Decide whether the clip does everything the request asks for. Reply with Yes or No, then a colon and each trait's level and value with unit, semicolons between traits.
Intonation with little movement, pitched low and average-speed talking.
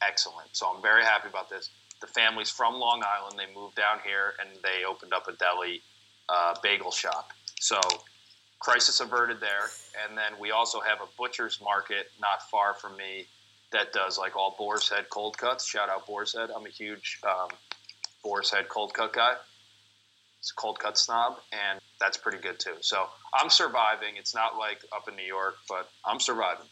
Yes: narrow, 2.2 semitones; low, 105 Hz; average, 190 wpm